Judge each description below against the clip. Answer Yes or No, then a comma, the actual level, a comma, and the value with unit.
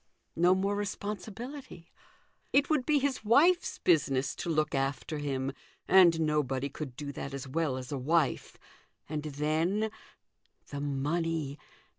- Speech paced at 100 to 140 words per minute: Yes, slow, 135 wpm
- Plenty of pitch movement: Yes, wide, 6.1 semitones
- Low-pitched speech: No, medium, 155 Hz